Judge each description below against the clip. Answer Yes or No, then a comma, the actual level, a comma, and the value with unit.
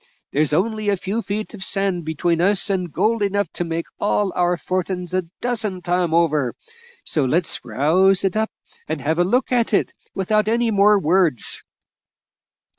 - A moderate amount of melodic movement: Yes, average, 3.5 semitones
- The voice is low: No, medium, 185 Hz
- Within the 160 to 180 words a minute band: Yes, average, 170 wpm